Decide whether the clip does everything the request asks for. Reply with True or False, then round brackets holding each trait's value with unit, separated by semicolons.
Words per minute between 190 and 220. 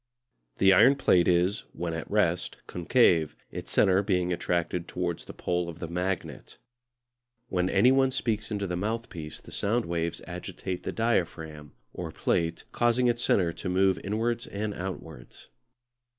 False (150 wpm)